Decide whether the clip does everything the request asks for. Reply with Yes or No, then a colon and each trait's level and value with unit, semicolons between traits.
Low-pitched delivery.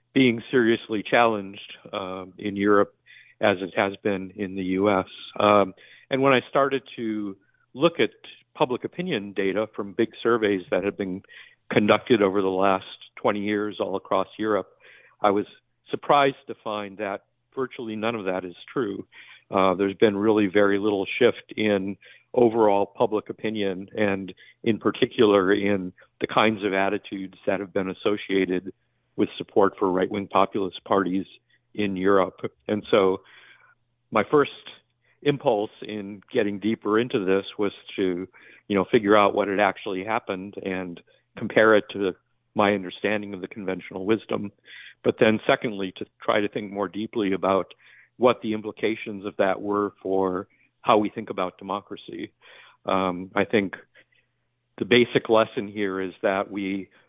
Yes: low, 100 Hz